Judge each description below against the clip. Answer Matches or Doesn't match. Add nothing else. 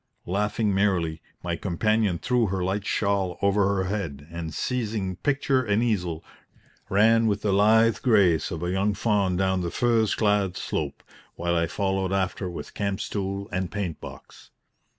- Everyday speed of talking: Matches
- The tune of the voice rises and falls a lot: Doesn't match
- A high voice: Doesn't match